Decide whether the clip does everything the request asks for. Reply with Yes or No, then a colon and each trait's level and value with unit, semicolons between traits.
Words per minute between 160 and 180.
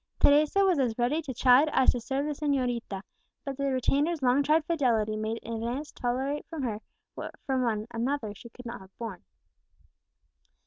Yes: average, 170 wpm